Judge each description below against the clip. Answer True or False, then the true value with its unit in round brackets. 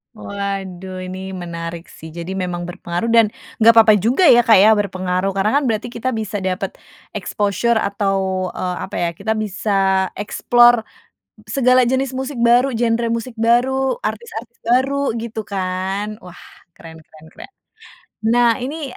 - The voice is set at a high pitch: True (210 Hz)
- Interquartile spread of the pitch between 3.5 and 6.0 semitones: True (4.0 semitones)